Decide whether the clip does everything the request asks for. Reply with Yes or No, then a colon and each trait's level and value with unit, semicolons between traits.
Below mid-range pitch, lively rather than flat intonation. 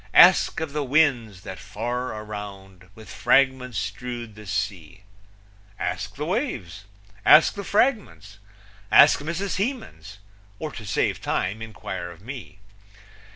Yes: low, 110 Hz; wide, 6.8 semitones